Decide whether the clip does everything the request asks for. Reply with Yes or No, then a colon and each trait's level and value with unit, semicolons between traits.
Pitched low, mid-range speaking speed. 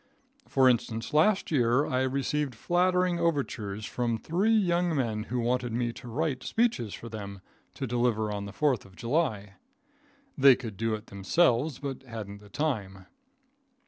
Yes: low, 125 Hz; average, 155 wpm